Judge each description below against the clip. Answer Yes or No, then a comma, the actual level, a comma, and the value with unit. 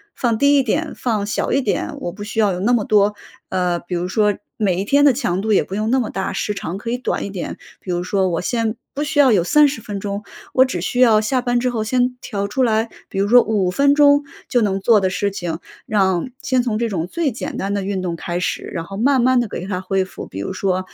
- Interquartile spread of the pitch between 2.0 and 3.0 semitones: No, average, 4.7 semitones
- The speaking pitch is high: Yes, high, 210 Hz